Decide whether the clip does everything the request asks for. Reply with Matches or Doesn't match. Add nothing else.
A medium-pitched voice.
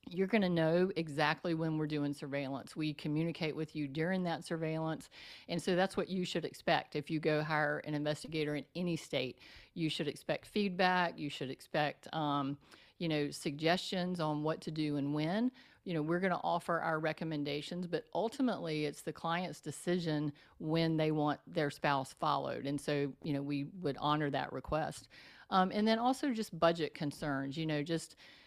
Matches